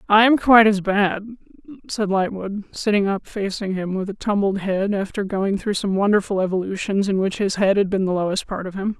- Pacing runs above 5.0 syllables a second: Yes, 5.5 syllables/s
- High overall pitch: Yes, high, 200 Hz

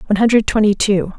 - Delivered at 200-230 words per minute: Yes, fast, 205 wpm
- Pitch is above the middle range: Yes, high, 210 Hz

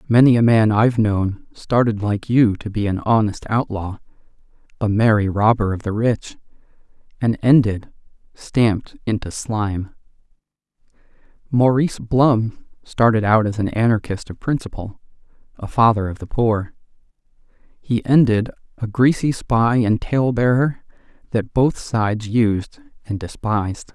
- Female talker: No, male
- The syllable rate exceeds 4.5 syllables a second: No, 4.4 syllables/s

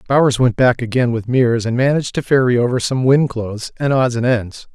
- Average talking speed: No, fast, 225 wpm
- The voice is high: No, low, 125 Hz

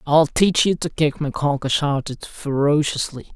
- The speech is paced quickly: No, average, 145 wpm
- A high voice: No, medium, 145 Hz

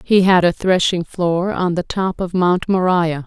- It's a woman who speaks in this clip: Yes, female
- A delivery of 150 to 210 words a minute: Yes, average, 200 wpm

